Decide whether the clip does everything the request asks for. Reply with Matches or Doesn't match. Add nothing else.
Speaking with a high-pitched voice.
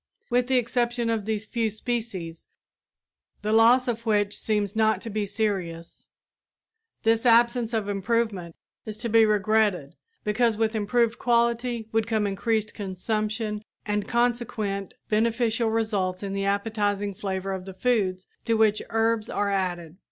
Matches